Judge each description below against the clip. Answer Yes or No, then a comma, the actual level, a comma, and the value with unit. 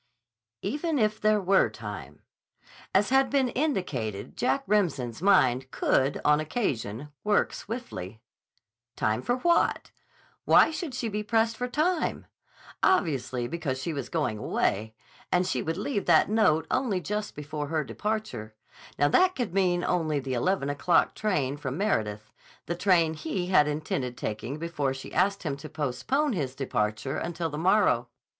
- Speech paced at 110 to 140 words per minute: No, average, 155 wpm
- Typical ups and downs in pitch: No, wide, 8.2 semitones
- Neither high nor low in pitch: Yes, medium, 165 Hz